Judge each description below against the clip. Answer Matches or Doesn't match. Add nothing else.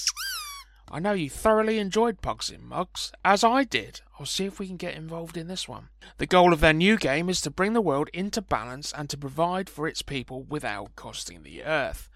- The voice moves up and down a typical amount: Doesn't match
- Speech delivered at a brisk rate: Matches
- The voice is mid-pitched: Matches